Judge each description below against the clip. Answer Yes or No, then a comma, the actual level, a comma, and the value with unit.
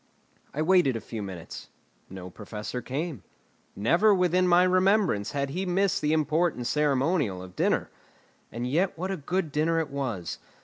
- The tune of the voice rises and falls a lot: Yes, wide, 7.2 semitones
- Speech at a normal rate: Yes, average, 160 wpm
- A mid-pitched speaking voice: Yes, medium, 150 Hz